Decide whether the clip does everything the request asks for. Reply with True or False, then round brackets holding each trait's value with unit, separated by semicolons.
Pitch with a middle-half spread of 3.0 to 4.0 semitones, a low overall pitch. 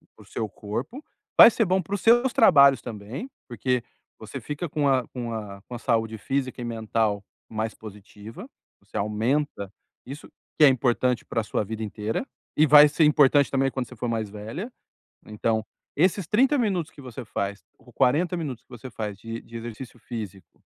False (5.2 semitones; 120 Hz)